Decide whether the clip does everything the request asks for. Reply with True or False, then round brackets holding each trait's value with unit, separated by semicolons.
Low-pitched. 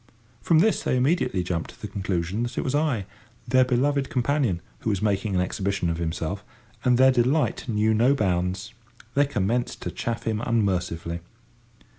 True (110 Hz)